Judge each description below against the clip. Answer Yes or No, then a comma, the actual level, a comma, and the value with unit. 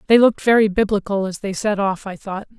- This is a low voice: No, high, 205 Hz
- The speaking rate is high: Yes, fast, 230 wpm